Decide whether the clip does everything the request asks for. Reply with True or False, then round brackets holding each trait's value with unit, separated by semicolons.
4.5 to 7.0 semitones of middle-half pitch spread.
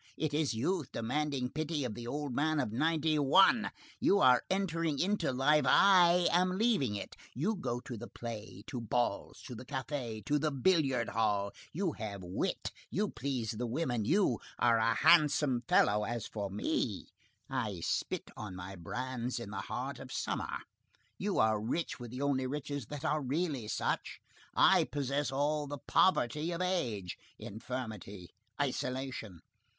True (5.0 semitones)